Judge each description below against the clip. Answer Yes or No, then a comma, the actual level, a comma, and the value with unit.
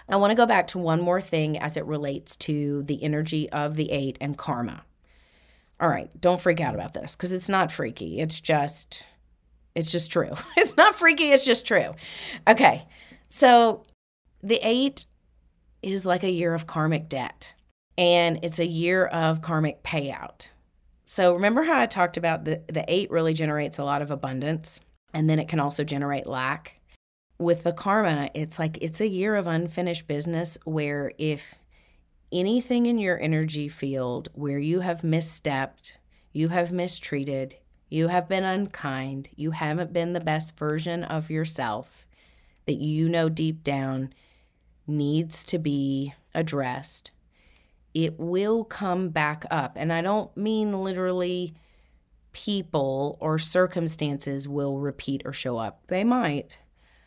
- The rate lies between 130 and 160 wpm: Yes, average, 155 wpm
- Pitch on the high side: No, medium, 160 Hz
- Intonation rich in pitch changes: No, average, 3.9 semitones